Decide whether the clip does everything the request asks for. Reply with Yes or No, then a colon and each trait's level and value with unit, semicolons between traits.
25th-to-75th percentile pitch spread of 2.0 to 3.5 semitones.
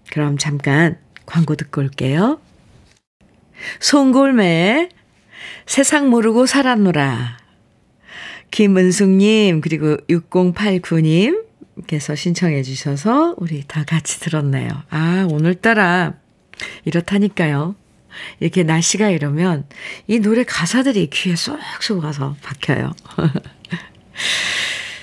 No: wide, 5.5 semitones